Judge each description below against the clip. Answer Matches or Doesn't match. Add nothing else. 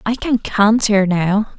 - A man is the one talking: Doesn't match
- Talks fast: Doesn't match